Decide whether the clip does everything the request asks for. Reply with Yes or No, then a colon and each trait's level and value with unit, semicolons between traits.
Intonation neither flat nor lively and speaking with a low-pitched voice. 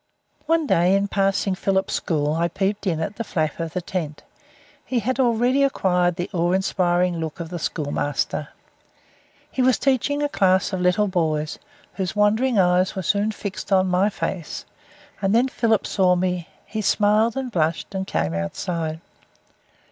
No: average, 3.7 semitones; high, 190 Hz